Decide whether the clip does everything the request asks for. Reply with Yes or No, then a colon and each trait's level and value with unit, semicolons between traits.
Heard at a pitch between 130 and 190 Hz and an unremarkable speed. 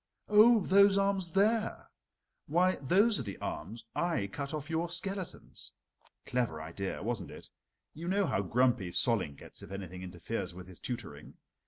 Yes: medium, 140 Hz; average, 155 wpm